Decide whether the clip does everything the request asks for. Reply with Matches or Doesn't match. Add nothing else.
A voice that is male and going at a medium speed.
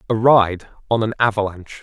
Matches